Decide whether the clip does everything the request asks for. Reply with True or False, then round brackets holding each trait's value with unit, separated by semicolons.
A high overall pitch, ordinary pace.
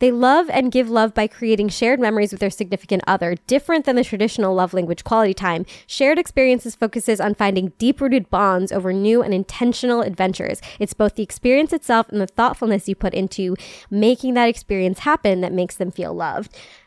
True (215 Hz; 190 wpm)